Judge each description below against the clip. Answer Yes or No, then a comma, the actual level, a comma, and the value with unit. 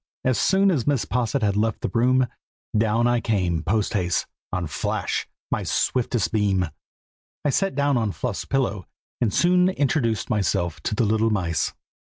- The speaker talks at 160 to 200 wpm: Yes, average, 165 wpm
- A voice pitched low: Yes, low, 115 Hz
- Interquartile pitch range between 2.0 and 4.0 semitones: No, average, 4.5 semitones